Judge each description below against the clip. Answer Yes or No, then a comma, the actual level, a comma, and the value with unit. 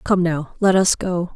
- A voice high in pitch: No, medium, 180 Hz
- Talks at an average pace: No, fast, 220 wpm